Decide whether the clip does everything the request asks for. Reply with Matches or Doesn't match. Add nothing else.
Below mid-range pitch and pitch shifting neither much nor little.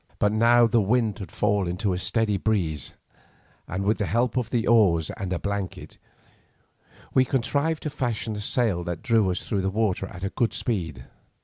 Matches